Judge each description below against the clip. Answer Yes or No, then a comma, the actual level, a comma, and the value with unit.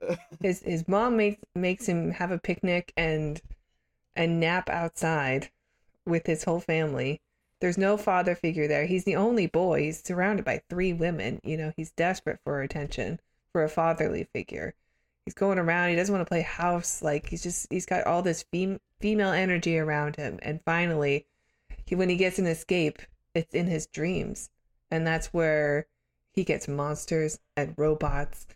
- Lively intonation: No, average, 2.9 semitones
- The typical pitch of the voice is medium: Yes, medium, 165 Hz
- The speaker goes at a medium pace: Yes, average, 170 wpm